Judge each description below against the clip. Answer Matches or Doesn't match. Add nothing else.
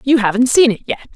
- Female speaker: Matches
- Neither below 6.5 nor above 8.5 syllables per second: Matches